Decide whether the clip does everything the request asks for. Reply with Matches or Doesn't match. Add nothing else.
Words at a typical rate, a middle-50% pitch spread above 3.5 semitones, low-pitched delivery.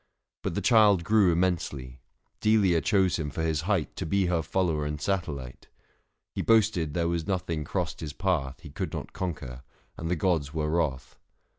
Matches